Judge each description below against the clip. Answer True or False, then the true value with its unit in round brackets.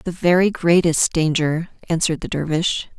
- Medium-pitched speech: True (165 Hz)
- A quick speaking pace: False (140 wpm)